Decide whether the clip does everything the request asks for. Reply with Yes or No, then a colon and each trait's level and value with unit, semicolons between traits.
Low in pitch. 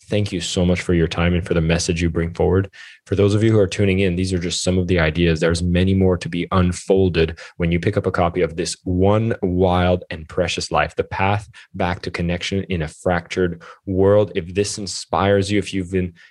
Yes: very low, 90 Hz